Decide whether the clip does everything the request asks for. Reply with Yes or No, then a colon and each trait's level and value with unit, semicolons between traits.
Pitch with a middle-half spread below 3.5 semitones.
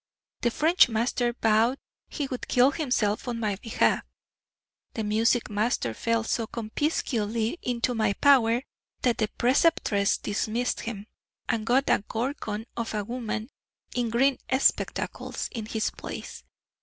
Yes: narrow, 2.4 semitones